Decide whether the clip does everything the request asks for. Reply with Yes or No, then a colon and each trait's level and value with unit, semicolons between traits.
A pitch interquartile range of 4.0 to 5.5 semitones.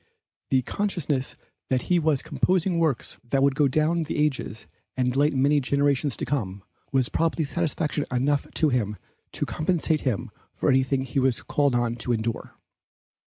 No: average, 3.4 semitones